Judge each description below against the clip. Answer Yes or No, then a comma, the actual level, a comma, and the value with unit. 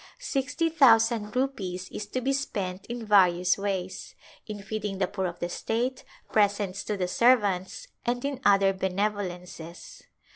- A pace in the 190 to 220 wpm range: No, average, 145 wpm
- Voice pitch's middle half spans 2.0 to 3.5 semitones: No, average, 4.4 semitones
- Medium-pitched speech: No, high, 205 Hz